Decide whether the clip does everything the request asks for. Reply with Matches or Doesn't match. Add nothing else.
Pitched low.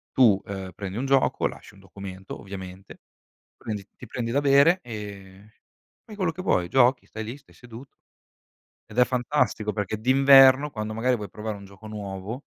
Matches